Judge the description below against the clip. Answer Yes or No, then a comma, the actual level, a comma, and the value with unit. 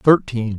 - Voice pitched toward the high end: No, low, 125 Hz